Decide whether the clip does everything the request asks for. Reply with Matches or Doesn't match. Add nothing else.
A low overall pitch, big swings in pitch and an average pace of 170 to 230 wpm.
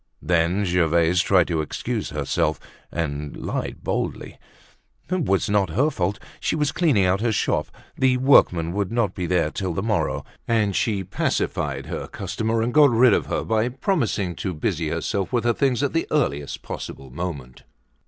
Matches